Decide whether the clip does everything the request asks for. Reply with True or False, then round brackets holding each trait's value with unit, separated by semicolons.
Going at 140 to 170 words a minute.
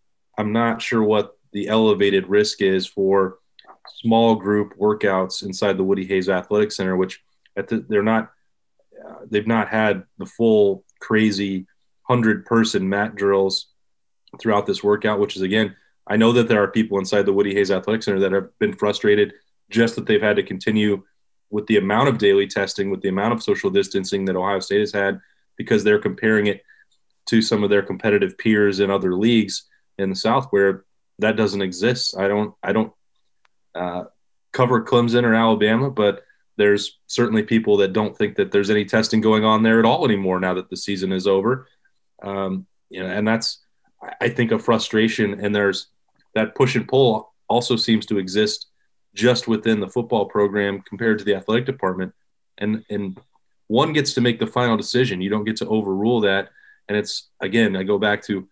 False (185 wpm)